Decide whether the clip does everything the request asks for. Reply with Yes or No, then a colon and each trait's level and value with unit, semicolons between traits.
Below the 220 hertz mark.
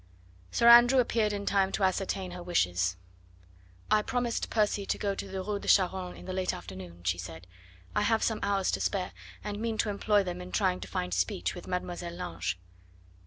Yes: high, 190 Hz